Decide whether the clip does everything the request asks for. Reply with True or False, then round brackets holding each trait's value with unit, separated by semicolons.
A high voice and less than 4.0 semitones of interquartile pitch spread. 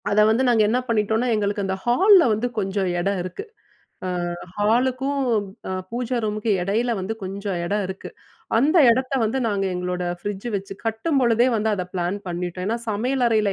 True (215 Hz; 3.6 semitones)